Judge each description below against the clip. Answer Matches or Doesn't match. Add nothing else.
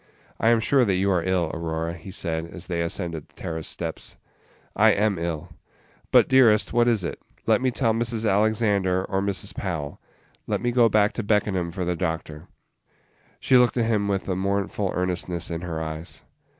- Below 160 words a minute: Doesn't match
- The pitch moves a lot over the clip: Doesn't match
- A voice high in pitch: Doesn't match